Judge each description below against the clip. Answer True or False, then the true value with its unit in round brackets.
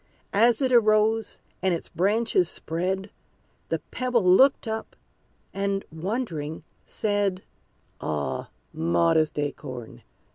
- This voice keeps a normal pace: False (100 wpm)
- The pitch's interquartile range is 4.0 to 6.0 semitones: True (5.6 semitones)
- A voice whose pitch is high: True (195 Hz)